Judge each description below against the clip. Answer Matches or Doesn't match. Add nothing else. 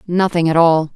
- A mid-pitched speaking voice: Matches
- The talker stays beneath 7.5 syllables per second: Matches